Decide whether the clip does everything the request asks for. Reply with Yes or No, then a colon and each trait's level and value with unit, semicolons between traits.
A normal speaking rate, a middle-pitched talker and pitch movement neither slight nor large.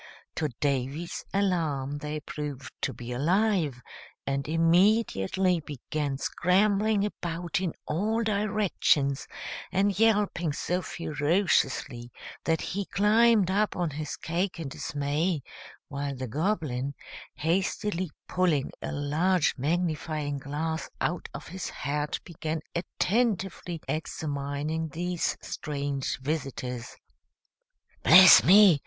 No: slow, 105 wpm; medium, 160 Hz; average, 4.7 semitones